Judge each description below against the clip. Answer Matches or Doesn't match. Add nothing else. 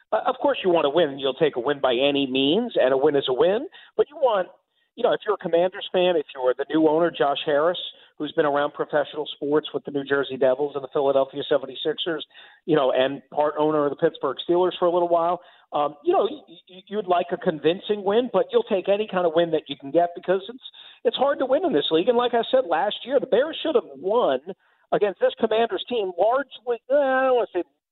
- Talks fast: Matches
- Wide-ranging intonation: Matches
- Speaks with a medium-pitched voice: Matches